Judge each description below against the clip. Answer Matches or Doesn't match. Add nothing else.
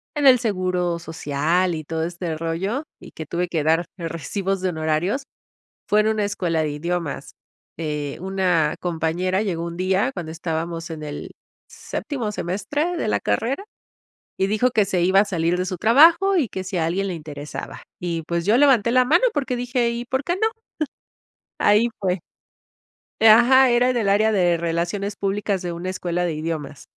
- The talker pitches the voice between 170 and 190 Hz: Matches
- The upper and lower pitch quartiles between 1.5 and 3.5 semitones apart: Doesn't match